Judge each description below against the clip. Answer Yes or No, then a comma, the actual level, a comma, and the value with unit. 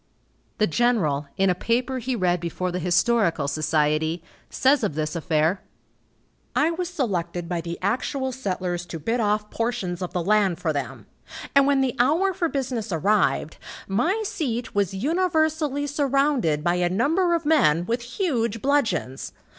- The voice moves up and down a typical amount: No, wide, 7.9 semitones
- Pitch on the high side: Yes, high, 215 Hz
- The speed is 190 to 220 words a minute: No, average, 155 wpm